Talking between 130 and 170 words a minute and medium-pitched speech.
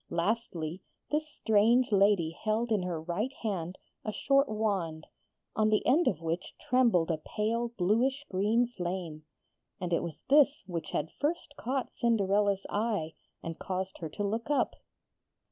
No: average, 150 wpm; high, 205 Hz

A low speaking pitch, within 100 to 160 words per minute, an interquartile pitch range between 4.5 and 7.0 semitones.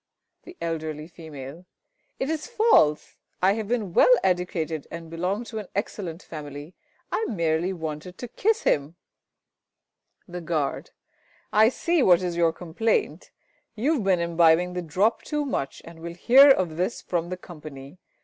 No: medium, 180 Hz; average, 155 wpm; average, 5.3 semitones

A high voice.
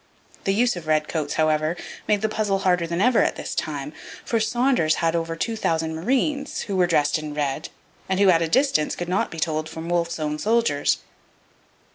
No: medium, 170 Hz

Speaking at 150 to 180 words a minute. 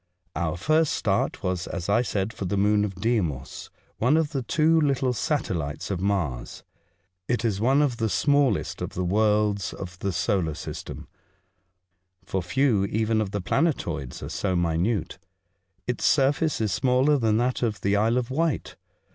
Yes: average, 170 wpm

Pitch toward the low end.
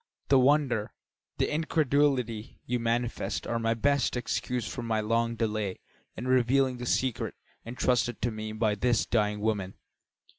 Yes: low, 120 Hz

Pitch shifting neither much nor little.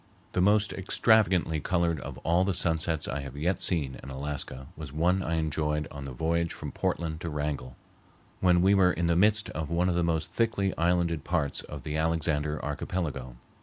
Yes: average, 3.3 semitones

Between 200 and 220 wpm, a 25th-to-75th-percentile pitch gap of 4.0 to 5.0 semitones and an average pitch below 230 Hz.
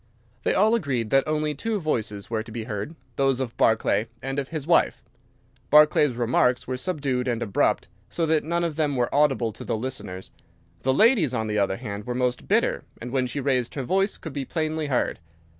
Yes: fast, 205 wpm; average, 4.6 semitones; low, 135 Hz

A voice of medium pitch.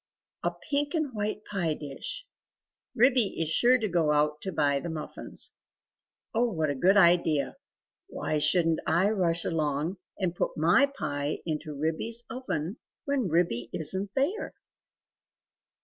Yes: medium, 175 Hz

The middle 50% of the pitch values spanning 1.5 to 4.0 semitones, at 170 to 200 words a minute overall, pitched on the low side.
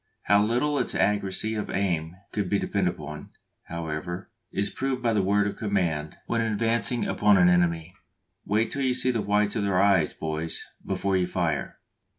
Yes: average, 3.6 semitones; average, 175 wpm; low, 100 Hz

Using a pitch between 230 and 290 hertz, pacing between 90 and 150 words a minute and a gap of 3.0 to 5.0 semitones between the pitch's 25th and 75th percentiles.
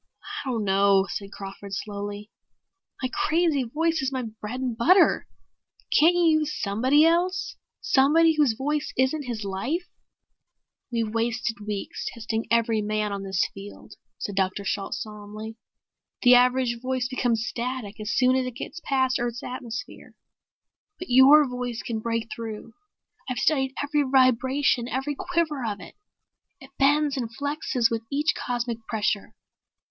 Yes: high, 245 Hz; average, 145 wpm; average, 4.3 semitones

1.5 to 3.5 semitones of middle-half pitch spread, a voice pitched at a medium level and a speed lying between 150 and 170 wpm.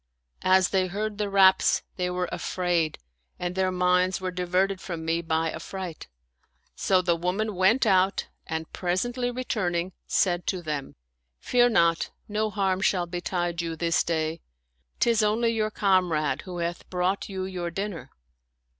Yes: narrow, 2.4 semitones; medium, 180 Hz; average, 155 wpm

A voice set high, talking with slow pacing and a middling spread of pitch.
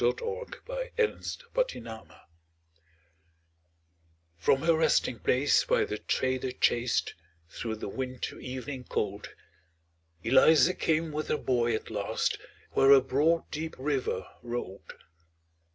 No: low, 135 Hz; slow, 115 wpm; average, 5.0 semitones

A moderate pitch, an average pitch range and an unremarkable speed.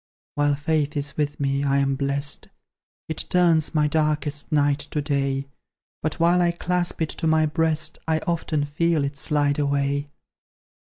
No: medium, 150 Hz; narrow, 2.0 semitones; average, 160 wpm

